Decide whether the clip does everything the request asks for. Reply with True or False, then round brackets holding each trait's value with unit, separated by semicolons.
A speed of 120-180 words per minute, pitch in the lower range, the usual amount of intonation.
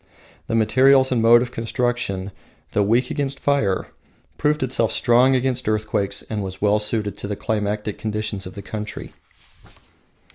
True (150 wpm; 110 Hz; 3.4 semitones)